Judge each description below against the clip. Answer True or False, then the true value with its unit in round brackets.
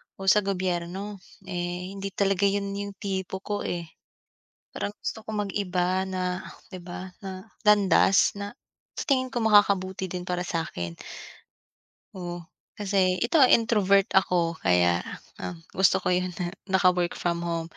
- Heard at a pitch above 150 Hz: True (190 Hz)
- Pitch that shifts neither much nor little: False (2.1 semitones)